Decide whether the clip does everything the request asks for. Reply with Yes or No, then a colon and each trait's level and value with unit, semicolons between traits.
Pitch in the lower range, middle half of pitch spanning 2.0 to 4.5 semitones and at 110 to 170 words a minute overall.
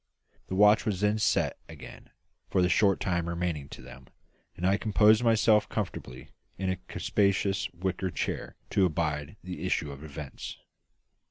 Yes: very low, 95 Hz; average, 3.8 semitones; average, 160 wpm